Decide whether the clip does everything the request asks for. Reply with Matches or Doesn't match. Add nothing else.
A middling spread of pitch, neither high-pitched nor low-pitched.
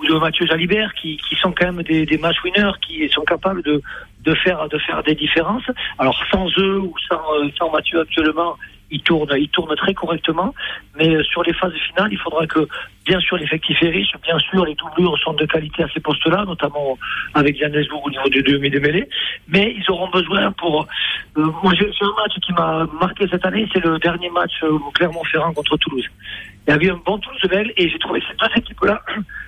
Matches